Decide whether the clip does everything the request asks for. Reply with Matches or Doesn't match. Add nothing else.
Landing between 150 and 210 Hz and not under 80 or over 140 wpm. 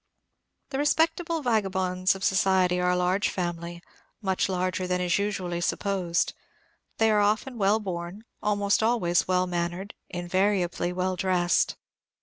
Matches